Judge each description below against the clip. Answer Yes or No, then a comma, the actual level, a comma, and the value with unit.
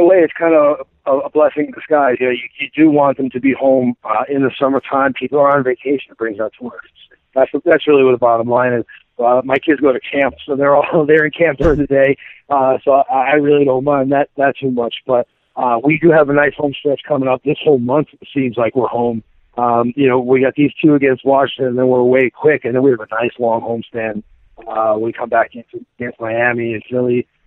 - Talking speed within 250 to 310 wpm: Yes, fast, 255 wpm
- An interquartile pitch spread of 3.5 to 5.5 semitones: No, average, 2.9 semitones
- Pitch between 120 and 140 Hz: Yes, low, 135 Hz